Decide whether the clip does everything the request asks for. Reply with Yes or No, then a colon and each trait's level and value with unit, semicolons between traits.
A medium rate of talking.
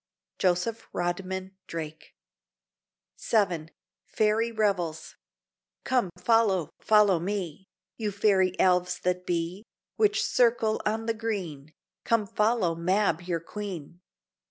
No: slow, 105 wpm